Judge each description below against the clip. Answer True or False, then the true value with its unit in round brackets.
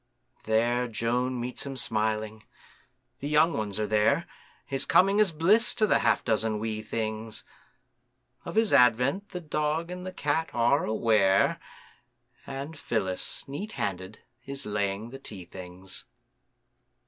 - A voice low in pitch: True (120 Hz)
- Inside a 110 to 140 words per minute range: True (135 wpm)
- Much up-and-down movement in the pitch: True (5.7 semitones)